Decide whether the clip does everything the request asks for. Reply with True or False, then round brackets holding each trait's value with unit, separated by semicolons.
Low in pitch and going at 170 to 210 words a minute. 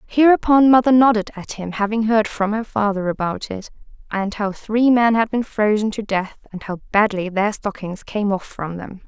False (210 Hz; 200 wpm)